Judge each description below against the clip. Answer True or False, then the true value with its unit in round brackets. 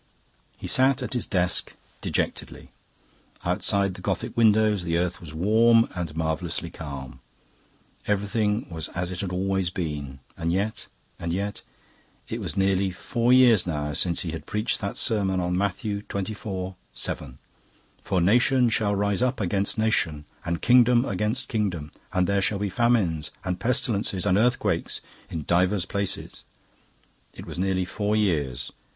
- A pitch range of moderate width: True (3.8 semitones)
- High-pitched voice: False (95 Hz)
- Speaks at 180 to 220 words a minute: False (145 wpm)